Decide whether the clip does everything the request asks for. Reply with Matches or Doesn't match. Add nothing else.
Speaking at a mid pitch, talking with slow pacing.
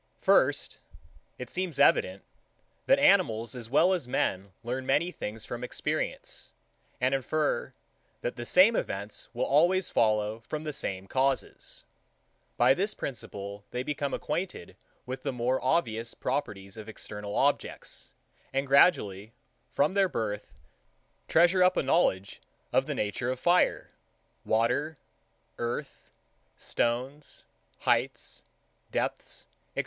Doesn't match